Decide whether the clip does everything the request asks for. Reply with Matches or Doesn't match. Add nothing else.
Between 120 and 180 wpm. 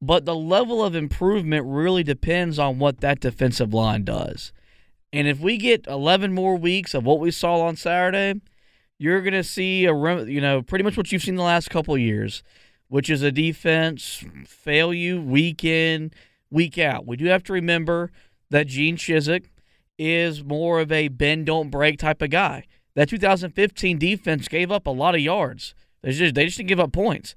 Doesn't match